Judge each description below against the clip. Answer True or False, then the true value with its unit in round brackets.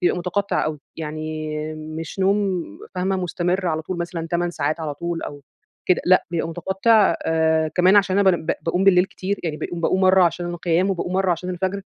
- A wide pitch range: False (2.6 semitones)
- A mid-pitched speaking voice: True (175 Hz)